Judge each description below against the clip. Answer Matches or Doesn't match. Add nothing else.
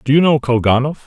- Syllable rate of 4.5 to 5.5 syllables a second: Doesn't match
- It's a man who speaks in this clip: Matches